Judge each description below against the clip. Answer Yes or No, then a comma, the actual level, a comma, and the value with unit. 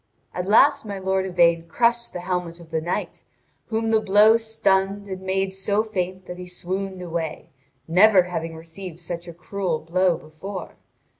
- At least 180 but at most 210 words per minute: No, average, 165 wpm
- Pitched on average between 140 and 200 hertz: Yes, medium, 185 Hz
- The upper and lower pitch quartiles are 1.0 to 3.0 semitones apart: Yes, average, 2.7 semitones